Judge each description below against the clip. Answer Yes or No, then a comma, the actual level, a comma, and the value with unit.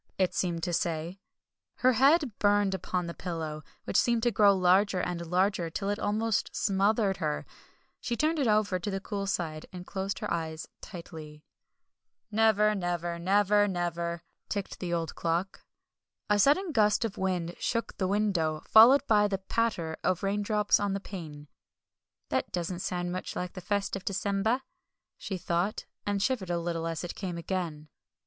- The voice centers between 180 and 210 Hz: Yes, high, 190 Hz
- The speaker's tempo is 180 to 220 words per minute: No, average, 170 wpm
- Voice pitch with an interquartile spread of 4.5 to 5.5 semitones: No, average, 3.3 semitones